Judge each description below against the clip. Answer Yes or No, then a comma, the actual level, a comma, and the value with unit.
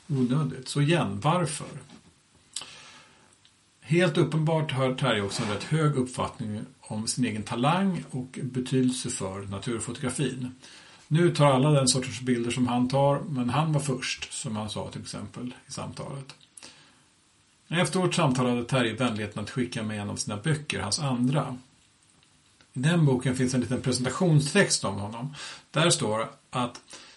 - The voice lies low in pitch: Yes, low, 130 Hz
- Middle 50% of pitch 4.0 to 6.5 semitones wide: No, average, 3.2 semitones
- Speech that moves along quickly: No, average, 150 wpm